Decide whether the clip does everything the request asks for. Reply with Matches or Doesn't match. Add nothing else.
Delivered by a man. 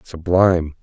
Matches